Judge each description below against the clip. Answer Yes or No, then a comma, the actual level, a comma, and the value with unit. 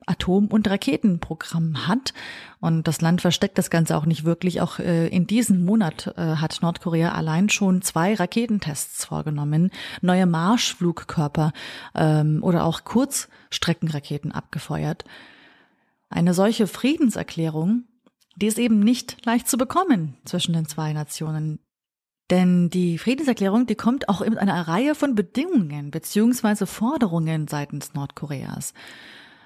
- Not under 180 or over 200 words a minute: No, slow, 125 wpm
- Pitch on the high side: No, medium, 180 Hz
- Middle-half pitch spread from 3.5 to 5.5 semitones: Yes, average, 5.1 semitones